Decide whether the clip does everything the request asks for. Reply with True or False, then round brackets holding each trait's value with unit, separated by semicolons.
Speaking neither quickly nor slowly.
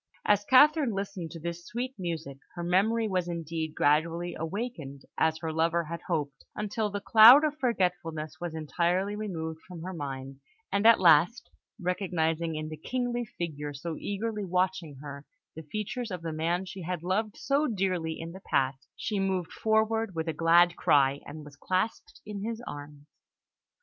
True (170 wpm)